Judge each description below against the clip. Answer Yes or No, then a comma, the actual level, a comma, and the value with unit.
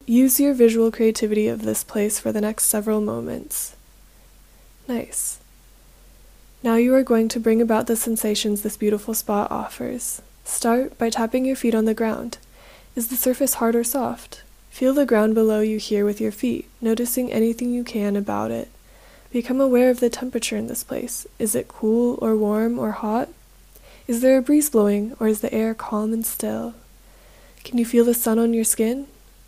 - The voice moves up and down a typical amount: No, narrow, 2.1 semitones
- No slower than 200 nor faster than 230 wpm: No, average, 185 wpm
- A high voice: Yes, high, 230 Hz